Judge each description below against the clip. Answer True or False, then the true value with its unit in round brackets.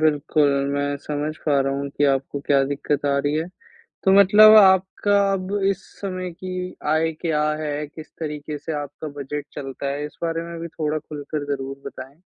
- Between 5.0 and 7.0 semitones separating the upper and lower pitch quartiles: False (2.9 semitones)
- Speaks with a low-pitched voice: False (150 Hz)